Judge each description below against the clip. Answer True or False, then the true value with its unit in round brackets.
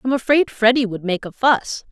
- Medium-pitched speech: False (235 Hz)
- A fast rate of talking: True (220 wpm)